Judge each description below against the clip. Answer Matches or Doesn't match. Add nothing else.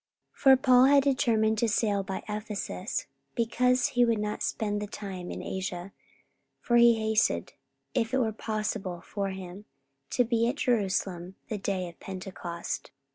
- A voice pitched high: Matches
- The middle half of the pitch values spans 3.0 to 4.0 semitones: Matches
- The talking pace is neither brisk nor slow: Matches